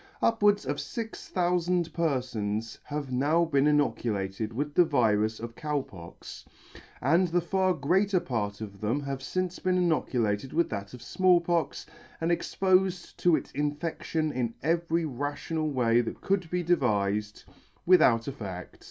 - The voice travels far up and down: Yes, wide, 7.0 semitones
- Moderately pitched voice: Yes, medium, 145 Hz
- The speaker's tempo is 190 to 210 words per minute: No, average, 150 wpm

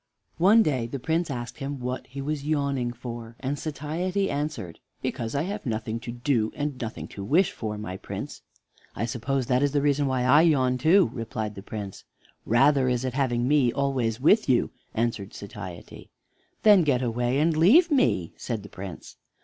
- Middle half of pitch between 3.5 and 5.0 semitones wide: Yes, average, 4.3 semitones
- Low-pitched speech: Yes, low, 130 Hz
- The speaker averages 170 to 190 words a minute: Yes, average, 180 wpm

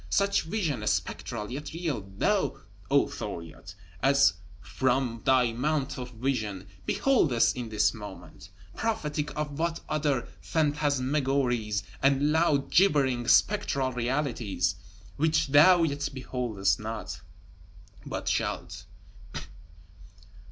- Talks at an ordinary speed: No, slow, 100 wpm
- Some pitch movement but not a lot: Yes, average, 4.8 semitones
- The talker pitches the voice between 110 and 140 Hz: Yes, low, 135 Hz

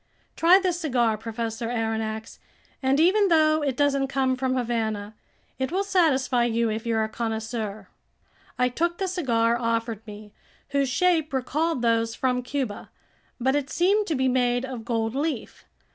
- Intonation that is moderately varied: Yes, average, 4.4 semitones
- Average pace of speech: Yes, average, 160 wpm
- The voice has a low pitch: No, very high, 250 Hz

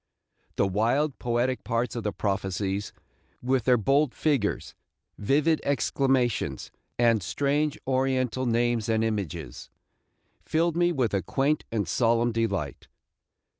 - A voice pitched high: No, low, 120 Hz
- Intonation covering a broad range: No, average, 4.3 semitones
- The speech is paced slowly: Yes, slow, 120 wpm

